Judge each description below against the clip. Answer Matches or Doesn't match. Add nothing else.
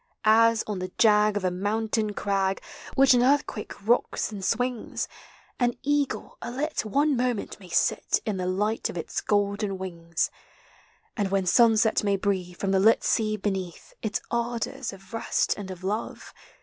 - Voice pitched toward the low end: Doesn't match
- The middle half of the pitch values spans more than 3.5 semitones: Doesn't match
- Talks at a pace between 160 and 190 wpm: Matches